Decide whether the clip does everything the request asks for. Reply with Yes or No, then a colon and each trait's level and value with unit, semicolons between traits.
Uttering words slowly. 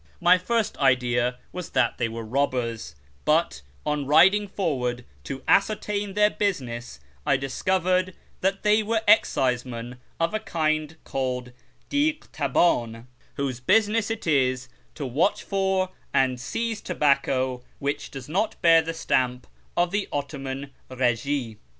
Yes: slow, 130 wpm